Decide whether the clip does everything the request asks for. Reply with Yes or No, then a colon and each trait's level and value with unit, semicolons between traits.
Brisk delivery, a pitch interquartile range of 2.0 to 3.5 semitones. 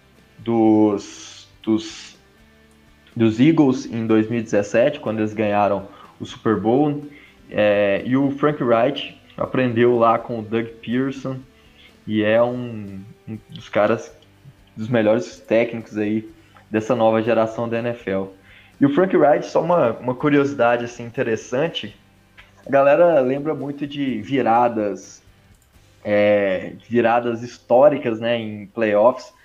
No: slow, 120 wpm; average, 3.1 semitones